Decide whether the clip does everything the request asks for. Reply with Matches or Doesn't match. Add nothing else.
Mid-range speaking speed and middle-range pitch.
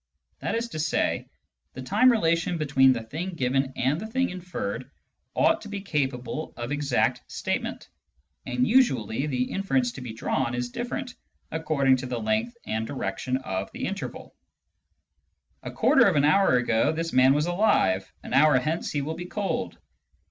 Matches